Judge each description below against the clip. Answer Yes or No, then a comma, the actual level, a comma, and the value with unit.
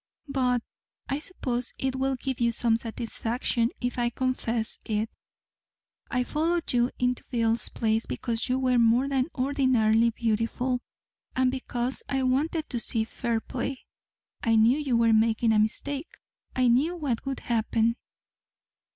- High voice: Yes, high, 245 Hz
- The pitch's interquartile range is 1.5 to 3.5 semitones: Yes, narrow, 2.4 semitones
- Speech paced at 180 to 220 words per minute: No, average, 145 wpm